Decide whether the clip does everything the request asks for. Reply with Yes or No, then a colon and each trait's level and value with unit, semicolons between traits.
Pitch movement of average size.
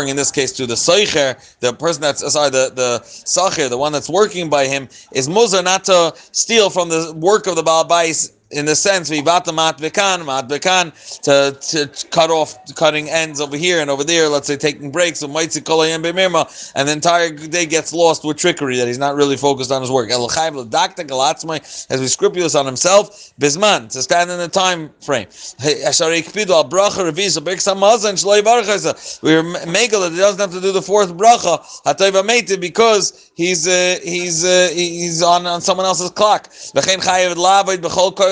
Yes: average, 4.0 semitones